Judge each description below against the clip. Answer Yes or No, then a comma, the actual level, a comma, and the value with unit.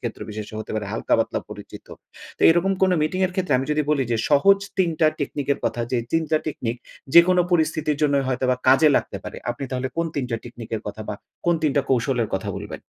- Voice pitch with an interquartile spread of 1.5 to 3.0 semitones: No, average, 5.1 semitones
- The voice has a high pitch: No, medium, 140 Hz